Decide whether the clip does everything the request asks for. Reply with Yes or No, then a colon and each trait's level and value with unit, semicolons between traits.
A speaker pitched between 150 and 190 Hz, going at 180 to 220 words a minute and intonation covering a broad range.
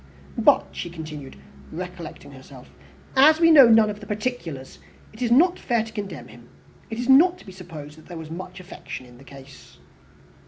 Yes: medium, 185 Hz; average, 190 wpm; wide, 7.8 semitones